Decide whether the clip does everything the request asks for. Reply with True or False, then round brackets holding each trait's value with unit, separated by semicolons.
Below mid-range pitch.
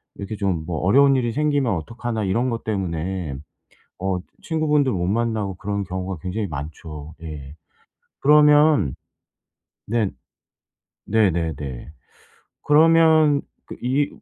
True (105 Hz)